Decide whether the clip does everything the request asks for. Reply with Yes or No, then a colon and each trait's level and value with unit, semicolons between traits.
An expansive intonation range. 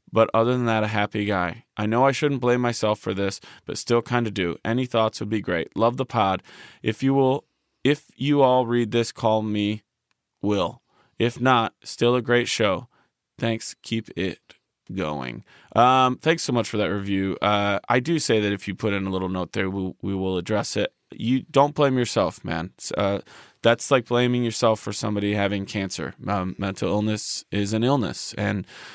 No: average, 3.4 semitones